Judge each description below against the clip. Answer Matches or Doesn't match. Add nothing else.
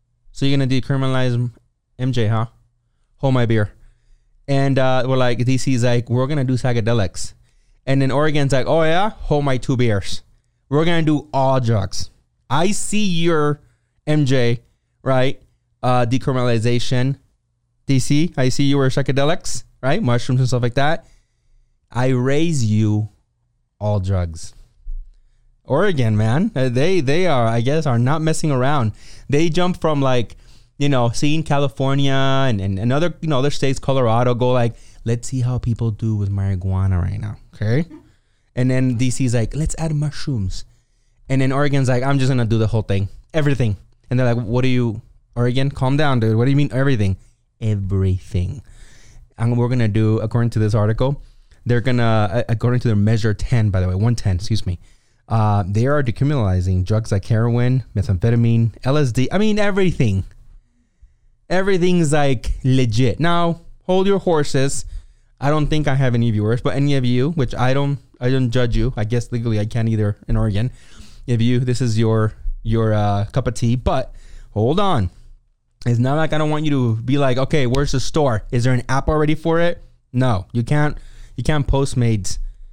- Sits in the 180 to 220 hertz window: Doesn't match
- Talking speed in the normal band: Matches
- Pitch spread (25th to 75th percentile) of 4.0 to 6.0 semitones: Doesn't match